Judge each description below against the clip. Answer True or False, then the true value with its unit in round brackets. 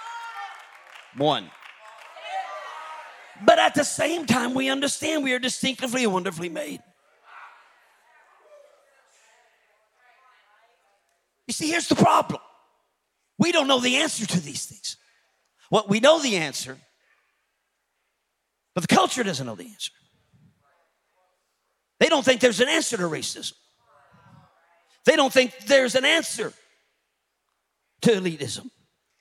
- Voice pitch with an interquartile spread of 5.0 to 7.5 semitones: True (5.3 semitones)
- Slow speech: True (115 wpm)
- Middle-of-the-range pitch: False (255 Hz)